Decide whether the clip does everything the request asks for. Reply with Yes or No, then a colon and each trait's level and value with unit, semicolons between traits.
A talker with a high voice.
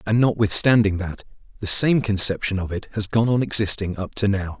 No: low, 105 Hz